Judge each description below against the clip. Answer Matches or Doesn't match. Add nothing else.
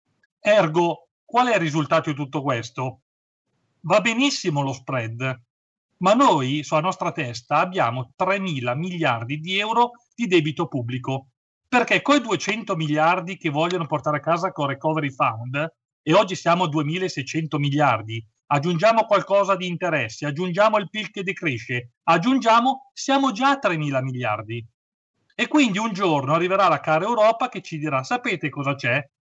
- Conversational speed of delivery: Matches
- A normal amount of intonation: Doesn't match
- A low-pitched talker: Doesn't match